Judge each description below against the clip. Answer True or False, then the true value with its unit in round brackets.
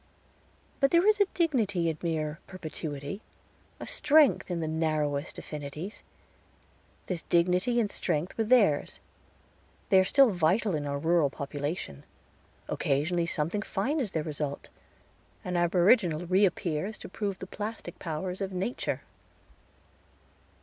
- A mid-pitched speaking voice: True (175 Hz)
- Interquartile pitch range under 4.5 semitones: False (5.1 semitones)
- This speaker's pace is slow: True (130 wpm)